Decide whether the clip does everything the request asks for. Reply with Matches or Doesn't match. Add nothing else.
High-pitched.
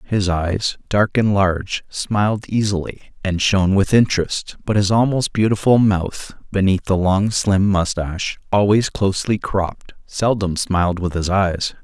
Doesn't match